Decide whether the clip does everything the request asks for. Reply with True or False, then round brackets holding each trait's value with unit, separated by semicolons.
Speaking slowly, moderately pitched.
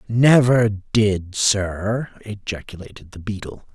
False (95 wpm; 105 Hz)